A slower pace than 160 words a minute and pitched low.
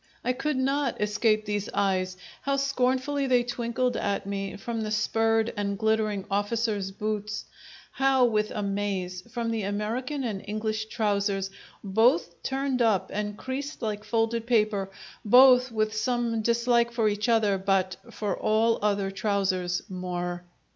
No: average, 140 wpm; high, 215 Hz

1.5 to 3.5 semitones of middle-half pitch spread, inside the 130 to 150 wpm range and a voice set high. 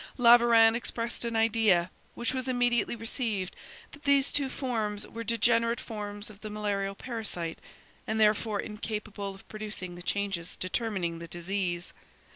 Yes: average, 2.9 semitones; average, 140 wpm; high, 215 Hz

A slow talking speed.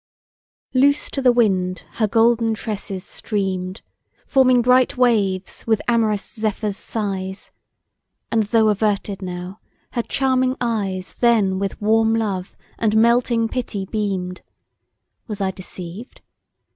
Yes: slow, 120 wpm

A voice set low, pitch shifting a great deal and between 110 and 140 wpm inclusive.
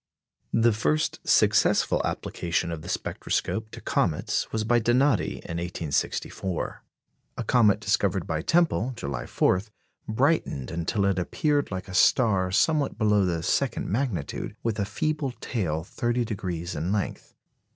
Yes: low, 105 Hz; wide, 5.7 semitones; slow, 135 wpm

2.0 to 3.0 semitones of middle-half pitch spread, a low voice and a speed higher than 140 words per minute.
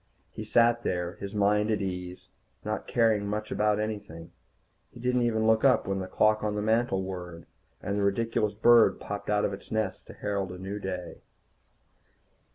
Yes: narrow, 2.4 semitones; low, 105 Hz; average, 180 wpm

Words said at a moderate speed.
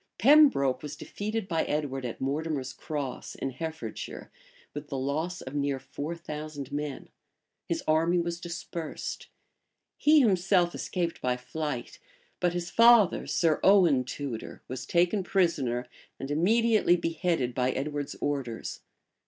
No: slow, 130 wpm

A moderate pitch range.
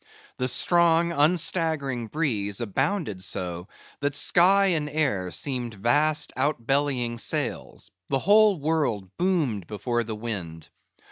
No: wide, 7.1 semitones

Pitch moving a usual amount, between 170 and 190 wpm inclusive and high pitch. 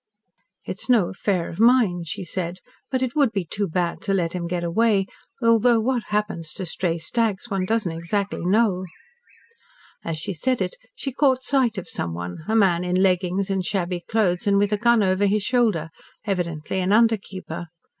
Yes: average, 4.4 semitones; average, 185 wpm; high, 195 Hz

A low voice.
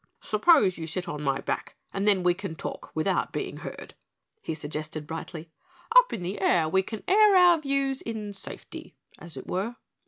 No: high, 190 Hz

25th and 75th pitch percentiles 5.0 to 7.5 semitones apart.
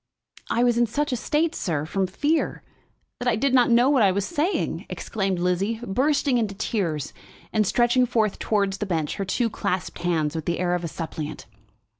Yes: wide, 5.4 semitones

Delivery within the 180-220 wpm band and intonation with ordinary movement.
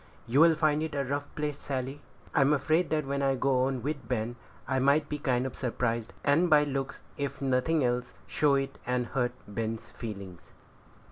Yes: average, 185 wpm; average, 3.0 semitones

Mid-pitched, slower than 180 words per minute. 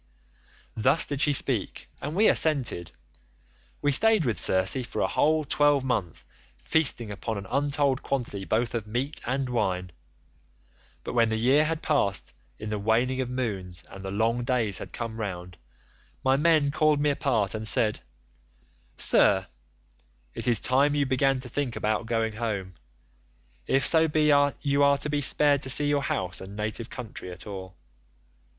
No: low, 125 Hz; average, 165 wpm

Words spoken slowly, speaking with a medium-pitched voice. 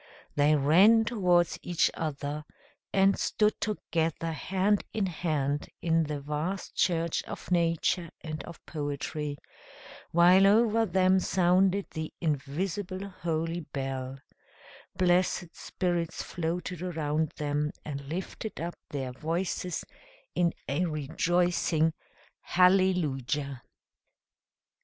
Yes: slow, 100 wpm; medium, 170 Hz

